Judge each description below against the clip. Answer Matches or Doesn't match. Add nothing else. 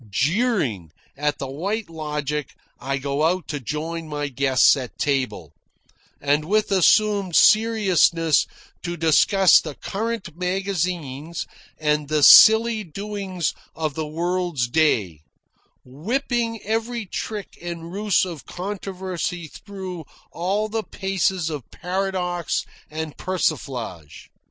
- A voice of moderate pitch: Matches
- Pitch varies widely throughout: Doesn't match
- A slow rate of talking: Matches